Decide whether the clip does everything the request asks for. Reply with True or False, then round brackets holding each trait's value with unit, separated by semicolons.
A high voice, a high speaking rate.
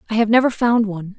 True (220 Hz; 250 wpm)